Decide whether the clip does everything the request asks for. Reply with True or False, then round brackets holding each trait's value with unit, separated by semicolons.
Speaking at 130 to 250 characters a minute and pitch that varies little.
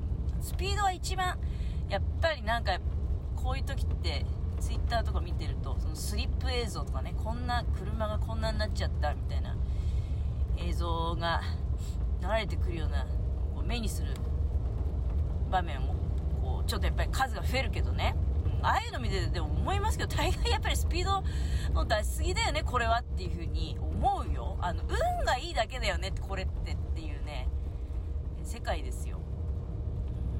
False (340 characters per minute; 1.9 semitones)